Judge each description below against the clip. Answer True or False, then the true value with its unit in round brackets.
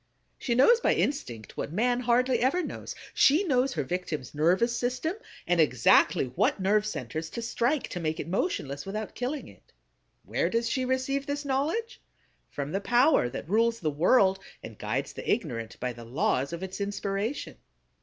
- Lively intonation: True (8.7 semitones)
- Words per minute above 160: True (175 wpm)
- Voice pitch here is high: True (210 Hz)